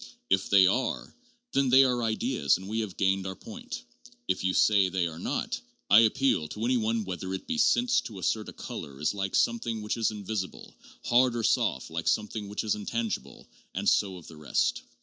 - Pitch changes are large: No, average, 3.9 semitones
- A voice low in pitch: Yes, low, 105 Hz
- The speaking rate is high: Yes, fast, 210 wpm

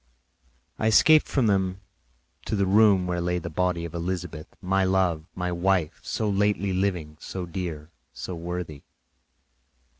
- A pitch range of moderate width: No, narrow, 2.2 semitones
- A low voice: Yes, very low, 90 Hz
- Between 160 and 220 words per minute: No, average, 145 wpm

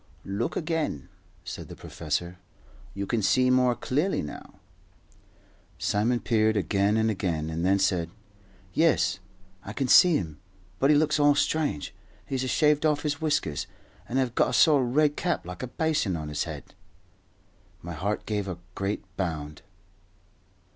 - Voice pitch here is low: Yes, low, 110 Hz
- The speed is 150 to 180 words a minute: Yes, average, 160 wpm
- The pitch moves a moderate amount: No, wide, 8.0 semitones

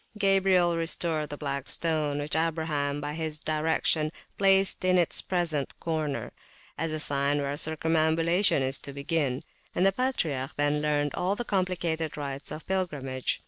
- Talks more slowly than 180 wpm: Yes, average, 150 wpm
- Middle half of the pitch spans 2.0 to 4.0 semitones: Yes, average, 3.0 semitones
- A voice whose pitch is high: No, medium, 155 Hz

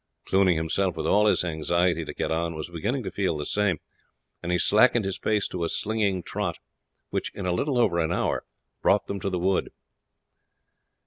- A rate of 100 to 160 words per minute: No, average, 190 wpm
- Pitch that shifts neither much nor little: Yes, average, 3.3 semitones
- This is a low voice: Yes, very low, 90 Hz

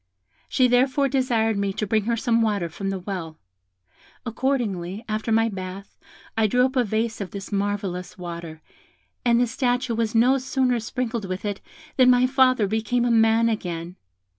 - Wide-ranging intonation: No, average, 3.9 semitones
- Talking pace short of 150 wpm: No, average, 170 wpm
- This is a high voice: Yes, high, 225 Hz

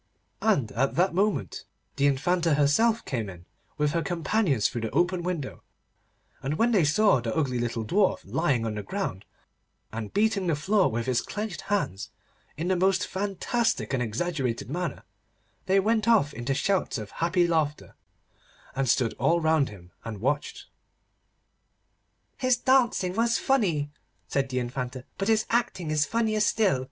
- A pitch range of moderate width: No, wide, 7.7 semitones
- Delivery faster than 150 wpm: Yes, average, 160 wpm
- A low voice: No, medium, 160 Hz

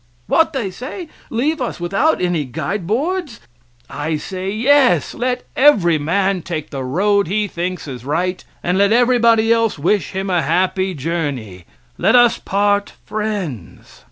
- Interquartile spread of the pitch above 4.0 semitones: Yes, wide, 5.6 semitones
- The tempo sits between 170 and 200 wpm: No, average, 150 wpm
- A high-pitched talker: Yes, high, 195 Hz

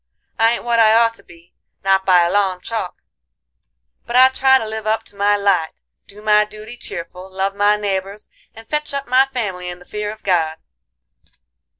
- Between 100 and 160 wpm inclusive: No, average, 195 wpm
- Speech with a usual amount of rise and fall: Yes, average, 3.2 semitones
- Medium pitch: No, high, 210 Hz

